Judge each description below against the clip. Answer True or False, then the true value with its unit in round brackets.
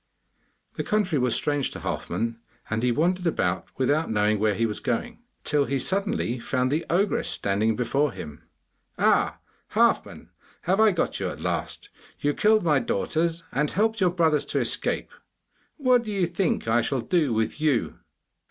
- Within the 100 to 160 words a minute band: False (170 wpm)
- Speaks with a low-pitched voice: False (150 Hz)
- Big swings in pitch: True (7.7 semitones)